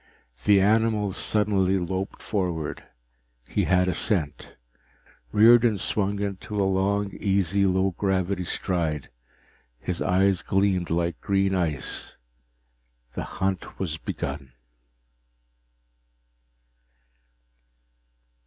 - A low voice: Yes, very low, 95 Hz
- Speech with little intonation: Yes, narrow, 2.2 semitones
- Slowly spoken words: Yes, slow, 90 wpm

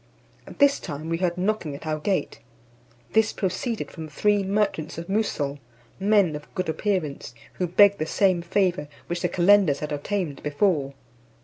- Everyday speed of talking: Yes, average, 165 wpm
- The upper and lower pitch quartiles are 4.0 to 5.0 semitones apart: Yes, average, 4.7 semitones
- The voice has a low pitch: No, medium, 180 Hz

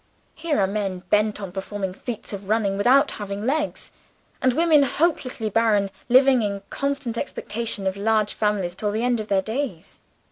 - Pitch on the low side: No, high, 215 Hz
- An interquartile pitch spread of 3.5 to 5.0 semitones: Yes, average, 4.1 semitones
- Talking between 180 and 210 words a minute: No, average, 170 wpm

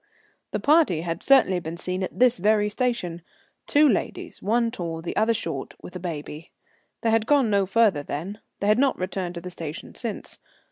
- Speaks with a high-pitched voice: Yes, high, 195 Hz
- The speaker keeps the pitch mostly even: No, average, 5.1 semitones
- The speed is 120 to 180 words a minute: No, average, 190 wpm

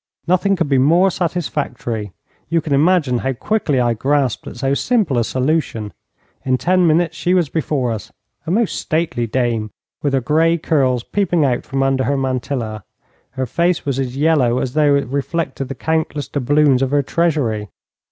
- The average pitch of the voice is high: No, medium, 140 Hz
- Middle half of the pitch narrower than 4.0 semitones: No, average, 4.4 semitones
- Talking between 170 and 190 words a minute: Yes, average, 175 wpm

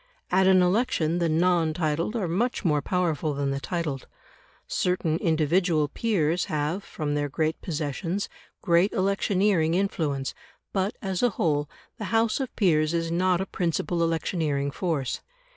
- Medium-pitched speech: Yes, medium, 170 Hz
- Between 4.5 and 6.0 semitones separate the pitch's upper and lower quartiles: No, average, 3.5 semitones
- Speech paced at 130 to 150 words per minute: Yes, average, 145 wpm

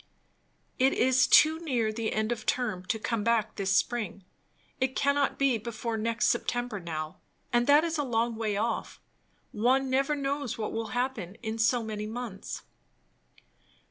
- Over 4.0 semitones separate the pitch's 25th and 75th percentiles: No, average, 3.2 semitones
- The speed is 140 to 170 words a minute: Yes, average, 160 wpm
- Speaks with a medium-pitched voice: No, high, 235 Hz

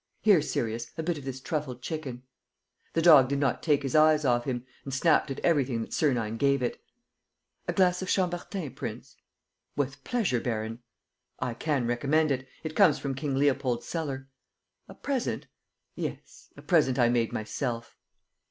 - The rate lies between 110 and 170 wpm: Yes, average, 165 wpm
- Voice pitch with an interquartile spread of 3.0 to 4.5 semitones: Yes, average, 4.1 semitones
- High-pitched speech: No, medium, 140 Hz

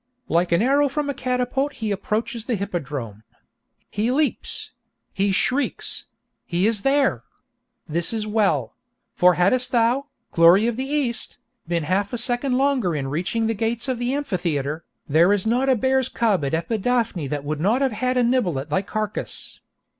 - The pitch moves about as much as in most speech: No, wide, 6.5 semitones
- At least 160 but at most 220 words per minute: Yes, average, 165 wpm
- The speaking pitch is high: Yes, high, 220 Hz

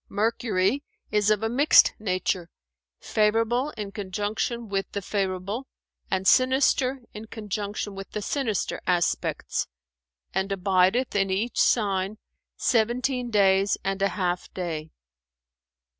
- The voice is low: No, high, 205 Hz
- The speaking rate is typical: No, slow, 115 wpm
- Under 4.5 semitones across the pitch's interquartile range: Yes, average, 3.2 semitones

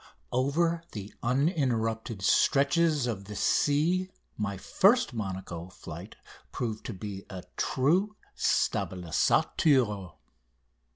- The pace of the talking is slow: Yes, slow, 100 wpm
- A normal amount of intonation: No, wide, 7.4 semitones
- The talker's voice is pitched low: Yes, low, 120 Hz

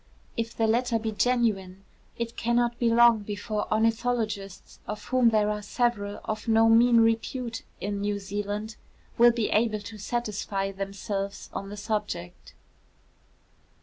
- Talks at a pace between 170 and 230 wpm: No, average, 140 wpm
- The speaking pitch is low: No, high, 220 Hz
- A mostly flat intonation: Yes, narrow, 2.3 semitones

